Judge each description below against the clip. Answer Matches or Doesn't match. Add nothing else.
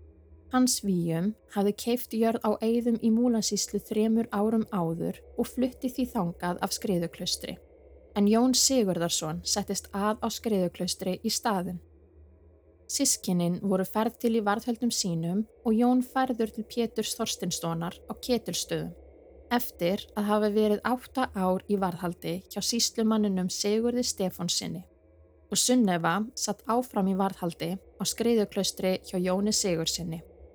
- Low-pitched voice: Doesn't match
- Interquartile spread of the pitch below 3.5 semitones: Doesn't match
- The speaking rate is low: Matches